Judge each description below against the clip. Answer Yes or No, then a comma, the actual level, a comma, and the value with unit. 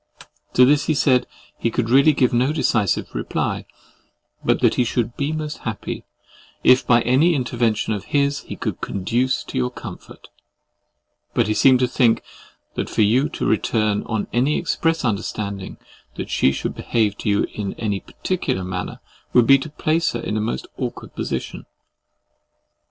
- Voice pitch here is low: Yes, low, 120 Hz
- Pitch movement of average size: Yes, average, 4.6 semitones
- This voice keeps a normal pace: Yes, average, 170 wpm